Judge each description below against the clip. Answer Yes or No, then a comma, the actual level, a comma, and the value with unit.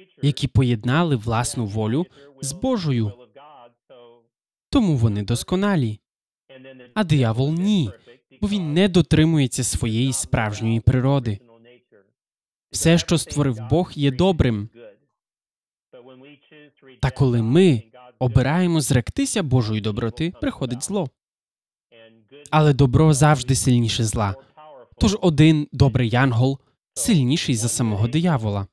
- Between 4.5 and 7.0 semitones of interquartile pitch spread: Yes, average, 4.8 semitones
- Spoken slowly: Yes, slow, 100 wpm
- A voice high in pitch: No, low, 135 Hz